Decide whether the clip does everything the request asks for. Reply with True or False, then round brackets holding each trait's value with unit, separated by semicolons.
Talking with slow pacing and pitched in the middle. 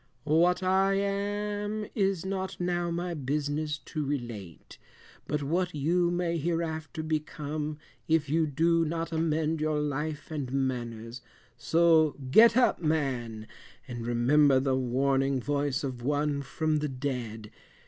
True (130 wpm; 150 Hz)